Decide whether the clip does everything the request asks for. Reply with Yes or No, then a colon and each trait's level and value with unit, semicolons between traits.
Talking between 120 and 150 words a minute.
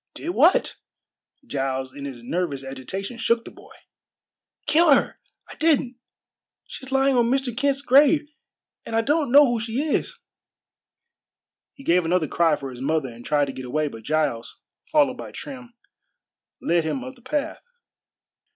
No: average, 160 wpm